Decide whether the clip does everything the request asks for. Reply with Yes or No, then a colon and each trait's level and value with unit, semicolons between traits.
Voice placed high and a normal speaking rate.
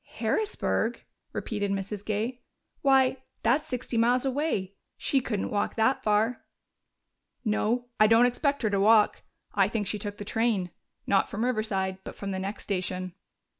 Yes: high, 220 Hz; average, 155 wpm